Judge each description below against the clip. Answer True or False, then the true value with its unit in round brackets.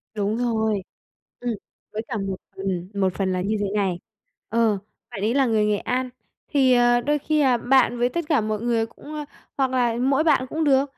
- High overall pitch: True (240 Hz)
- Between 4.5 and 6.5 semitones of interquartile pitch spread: False (4.0 semitones)